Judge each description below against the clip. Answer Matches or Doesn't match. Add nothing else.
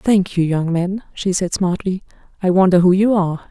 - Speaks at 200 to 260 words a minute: Matches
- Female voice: Matches